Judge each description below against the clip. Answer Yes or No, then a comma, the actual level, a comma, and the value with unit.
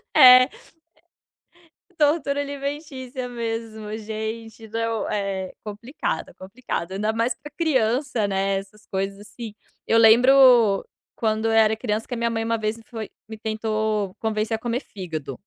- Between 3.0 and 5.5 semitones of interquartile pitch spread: No, narrow, 2.6 semitones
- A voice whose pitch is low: No, high, 225 Hz